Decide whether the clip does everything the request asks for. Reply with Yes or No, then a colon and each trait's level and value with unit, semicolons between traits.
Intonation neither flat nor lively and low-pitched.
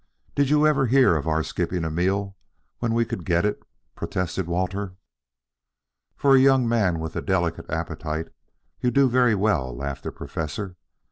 No: wide, 6.8 semitones; very low, 95 Hz